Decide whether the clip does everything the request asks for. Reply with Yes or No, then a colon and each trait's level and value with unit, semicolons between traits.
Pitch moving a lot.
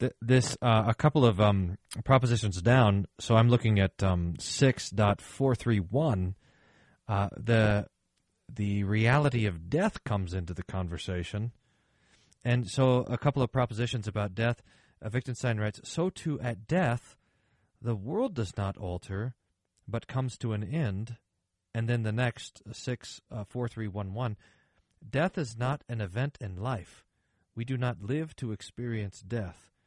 No: average, 3.8 semitones